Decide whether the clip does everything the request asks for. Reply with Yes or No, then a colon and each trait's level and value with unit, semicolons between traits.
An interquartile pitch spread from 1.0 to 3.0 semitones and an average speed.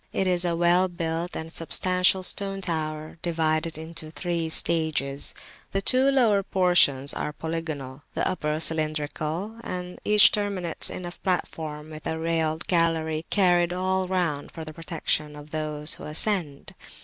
Yes: average, 2.7 semitones; average, 150 wpm